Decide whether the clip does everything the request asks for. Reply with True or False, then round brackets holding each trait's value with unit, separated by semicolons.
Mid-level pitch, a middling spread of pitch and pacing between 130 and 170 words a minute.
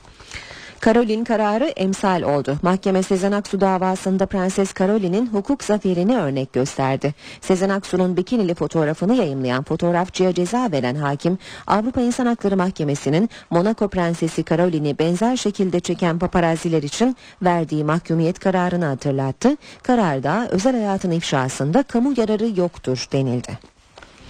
False (180 Hz; 5.0 semitones; 115 wpm)